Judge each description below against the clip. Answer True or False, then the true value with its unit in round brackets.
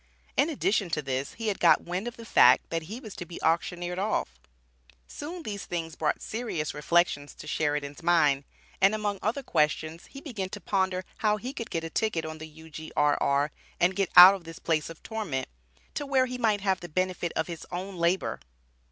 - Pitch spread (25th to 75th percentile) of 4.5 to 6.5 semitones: True (4.9 semitones)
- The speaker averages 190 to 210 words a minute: True (200 wpm)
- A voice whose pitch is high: False (175 Hz)